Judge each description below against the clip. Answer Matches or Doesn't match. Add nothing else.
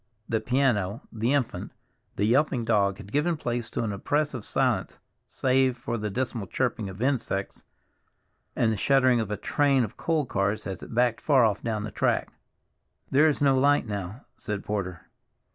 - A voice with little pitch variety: Doesn't match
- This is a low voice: Matches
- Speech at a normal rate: Matches